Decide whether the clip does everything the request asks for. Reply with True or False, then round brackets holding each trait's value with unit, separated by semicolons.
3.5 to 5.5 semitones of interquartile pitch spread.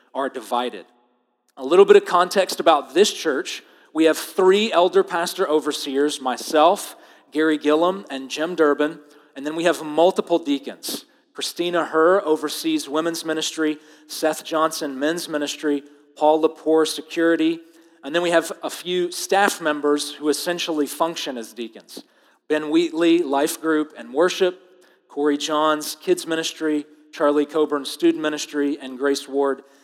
False (2.5 semitones)